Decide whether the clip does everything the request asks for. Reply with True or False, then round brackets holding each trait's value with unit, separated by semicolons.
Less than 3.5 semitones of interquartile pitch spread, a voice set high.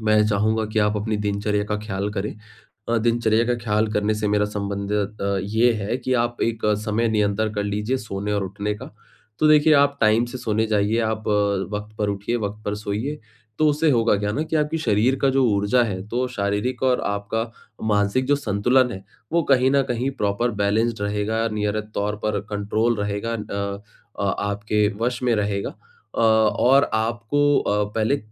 False (2.6 semitones; 110 Hz)